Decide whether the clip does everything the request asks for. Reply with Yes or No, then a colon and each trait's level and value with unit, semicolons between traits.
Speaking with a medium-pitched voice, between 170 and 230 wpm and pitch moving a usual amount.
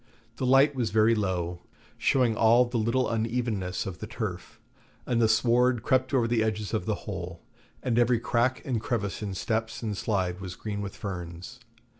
No: low, 110 Hz; average, 180 wpm; average, 3.3 semitones